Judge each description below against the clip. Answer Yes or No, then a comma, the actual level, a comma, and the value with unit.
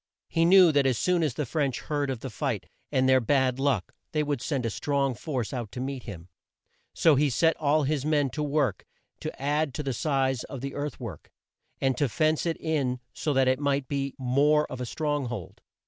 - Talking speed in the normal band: No, fast, 220 wpm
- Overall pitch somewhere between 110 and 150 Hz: Yes, medium, 140 Hz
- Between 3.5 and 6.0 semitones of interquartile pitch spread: No, average, 2.7 semitones